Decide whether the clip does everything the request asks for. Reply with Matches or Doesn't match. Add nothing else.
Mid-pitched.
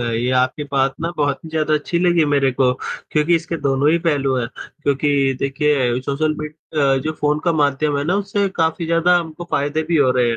Matches